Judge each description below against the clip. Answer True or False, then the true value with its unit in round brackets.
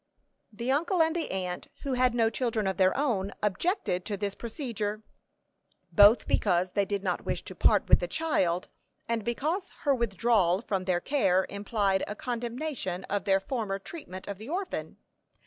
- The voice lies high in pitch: True (215 Hz)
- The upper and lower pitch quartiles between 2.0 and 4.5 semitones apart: False (5.0 semitones)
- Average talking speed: True (170 wpm)